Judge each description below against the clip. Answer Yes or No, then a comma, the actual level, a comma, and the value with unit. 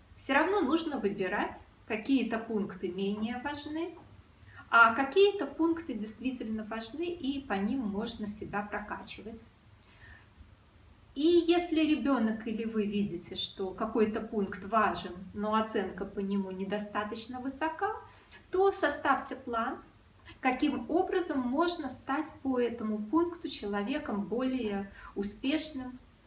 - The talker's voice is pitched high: Yes, high, 230 Hz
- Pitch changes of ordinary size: No, wide, 6.1 semitones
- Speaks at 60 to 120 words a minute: Yes, slow, 110 wpm